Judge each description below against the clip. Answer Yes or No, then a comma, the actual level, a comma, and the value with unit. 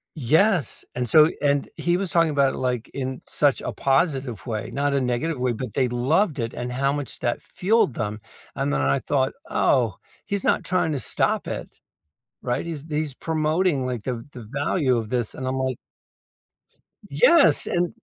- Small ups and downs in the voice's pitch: No, average, 4.2 semitones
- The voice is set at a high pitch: No, low, 135 Hz